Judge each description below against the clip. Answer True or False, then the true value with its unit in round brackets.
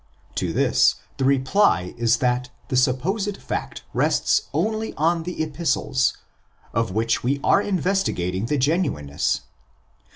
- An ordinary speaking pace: False (130 wpm)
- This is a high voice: False (135 Hz)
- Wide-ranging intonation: True (7.2 semitones)